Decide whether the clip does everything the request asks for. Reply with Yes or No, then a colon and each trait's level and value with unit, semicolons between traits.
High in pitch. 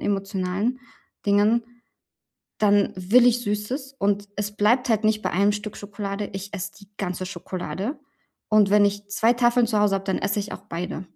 Yes: high, 205 Hz